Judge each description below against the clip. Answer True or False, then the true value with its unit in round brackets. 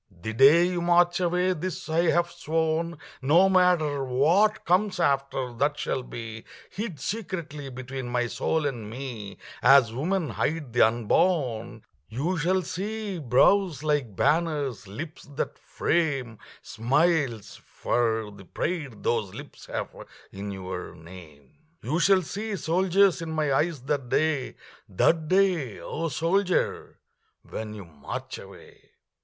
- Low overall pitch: False (150 Hz)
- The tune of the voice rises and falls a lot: True (6.5 semitones)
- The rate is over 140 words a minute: False (135 wpm)